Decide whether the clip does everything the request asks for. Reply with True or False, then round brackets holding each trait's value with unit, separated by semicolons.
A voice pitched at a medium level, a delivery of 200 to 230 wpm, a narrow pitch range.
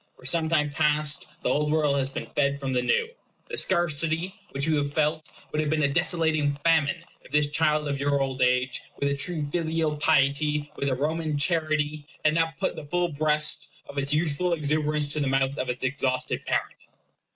True (150 Hz; 205 wpm; 2.0 semitones)